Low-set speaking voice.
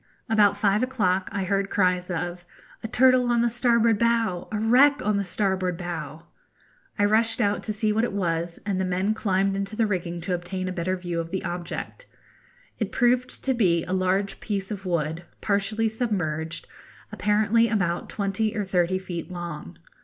No: high, 195 Hz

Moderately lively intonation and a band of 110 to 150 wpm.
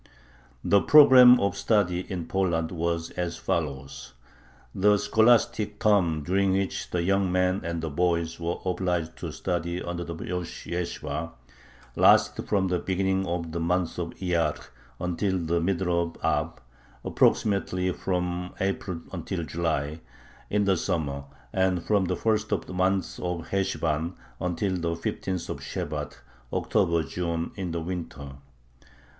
No: narrow, 2.3 semitones; average, 140 wpm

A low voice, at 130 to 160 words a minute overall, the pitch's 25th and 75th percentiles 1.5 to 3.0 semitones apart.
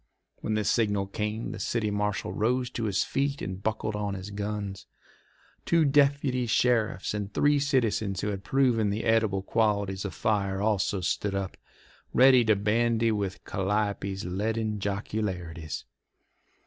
Yes: low, 105 Hz; average, 145 wpm; narrow, 2.6 semitones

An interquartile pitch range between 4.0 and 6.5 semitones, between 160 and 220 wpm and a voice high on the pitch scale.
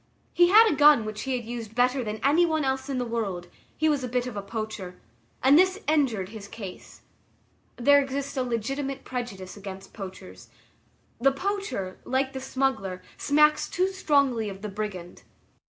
Yes: average, 5.2 semitones; average, 170 wpm; very high, 250 Hz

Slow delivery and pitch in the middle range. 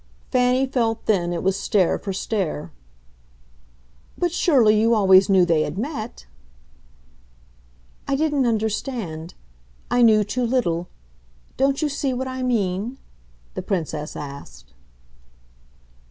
No: slow, 120 wpm; high, 215 Hz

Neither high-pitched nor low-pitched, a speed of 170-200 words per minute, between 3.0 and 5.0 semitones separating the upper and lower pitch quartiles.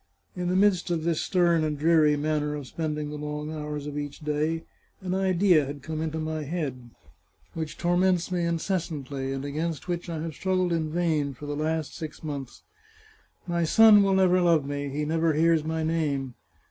No: medium, 160 Hz; average, 185 wpm; narrow, 2.5 semitones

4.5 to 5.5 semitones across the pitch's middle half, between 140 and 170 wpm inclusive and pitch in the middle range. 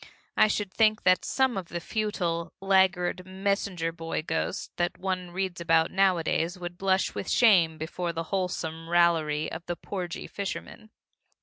No: narrow, 2.5 semitones; average, 150 wpm; medium, 180 Hz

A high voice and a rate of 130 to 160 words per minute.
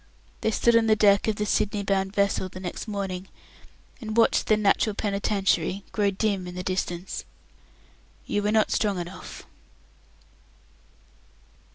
Yes: high, 200 Hz; average, 145 wpm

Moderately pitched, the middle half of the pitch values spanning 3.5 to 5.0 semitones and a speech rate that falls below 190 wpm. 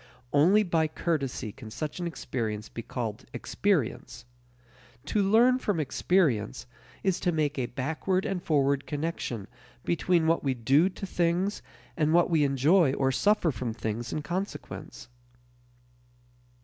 No: medium, 155 Hz; wide, 5.5 semitones; slow, 135 wpm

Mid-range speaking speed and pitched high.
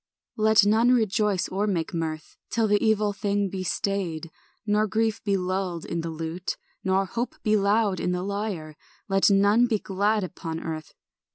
Yes: average, 170 wpm; high, 200 Hz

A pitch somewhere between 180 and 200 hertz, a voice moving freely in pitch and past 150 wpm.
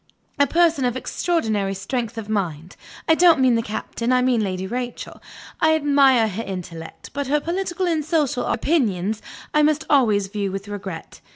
No: high, 245 Hz; wide, 6.8 semitones; average, 170 wpm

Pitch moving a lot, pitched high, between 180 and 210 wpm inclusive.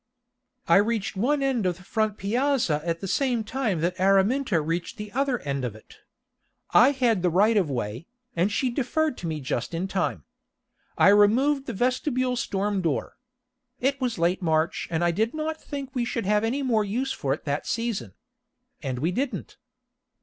Yes: wide, 6.9 semitones; high, 210 Hz; average, 185 wpm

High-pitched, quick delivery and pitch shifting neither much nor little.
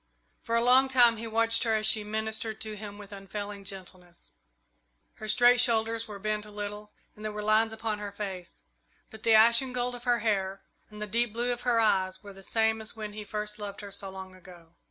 No: high, 215 Hz; fast, 220 wpm; narrow, 2.0 semitones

